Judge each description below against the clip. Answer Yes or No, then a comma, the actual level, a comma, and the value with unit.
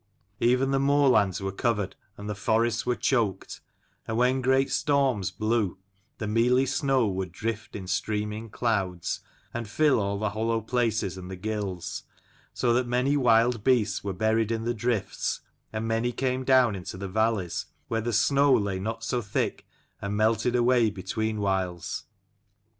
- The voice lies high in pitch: No, low, 110 Hz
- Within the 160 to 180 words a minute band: Yes, average, 165 wpm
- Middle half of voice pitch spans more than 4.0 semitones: No, average, 3.3 semitones